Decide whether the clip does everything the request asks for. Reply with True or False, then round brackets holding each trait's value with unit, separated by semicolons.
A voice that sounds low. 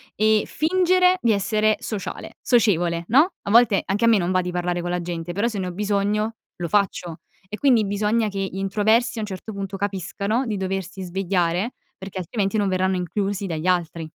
False (200 Hz)